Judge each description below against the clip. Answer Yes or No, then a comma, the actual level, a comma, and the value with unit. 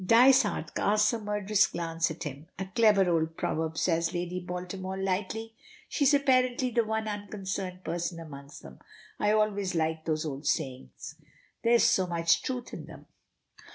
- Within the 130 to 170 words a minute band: Yes, average, 160 wpm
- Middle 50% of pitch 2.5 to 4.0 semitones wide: No, average, 4.6 semitones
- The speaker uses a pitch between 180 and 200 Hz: Yes, medium, 185 Hz